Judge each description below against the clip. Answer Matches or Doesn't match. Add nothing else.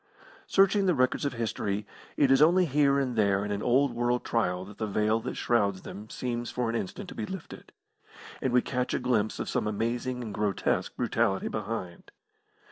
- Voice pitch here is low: Matches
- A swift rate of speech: Doesn't match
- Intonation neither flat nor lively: Matches